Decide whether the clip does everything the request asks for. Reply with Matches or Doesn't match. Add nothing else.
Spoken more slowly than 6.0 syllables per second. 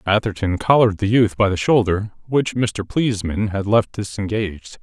Matches